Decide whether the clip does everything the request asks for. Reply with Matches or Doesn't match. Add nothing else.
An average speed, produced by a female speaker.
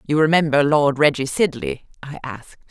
Matches